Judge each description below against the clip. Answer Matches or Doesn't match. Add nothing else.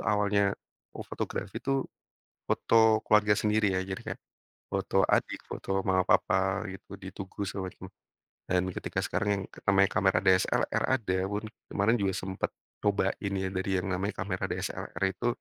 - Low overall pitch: Matches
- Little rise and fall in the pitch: Matches